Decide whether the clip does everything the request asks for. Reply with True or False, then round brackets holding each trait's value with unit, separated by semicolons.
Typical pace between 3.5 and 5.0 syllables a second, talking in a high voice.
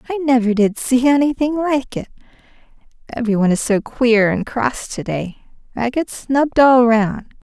True (4.8 syllables/s; 240 Hz)